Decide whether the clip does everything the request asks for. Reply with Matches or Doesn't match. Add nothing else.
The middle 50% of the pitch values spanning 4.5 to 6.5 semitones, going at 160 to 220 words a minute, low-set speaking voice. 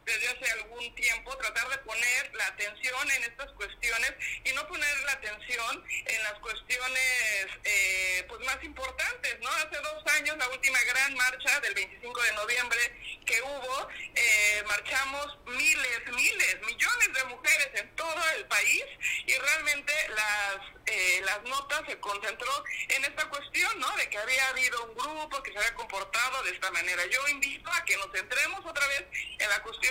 Doesn't match